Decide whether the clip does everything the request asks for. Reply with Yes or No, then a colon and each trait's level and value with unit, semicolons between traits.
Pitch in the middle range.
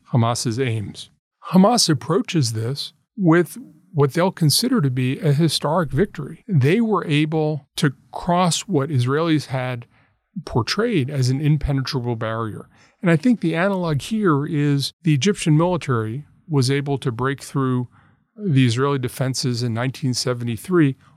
Yes: medium, 145 Hz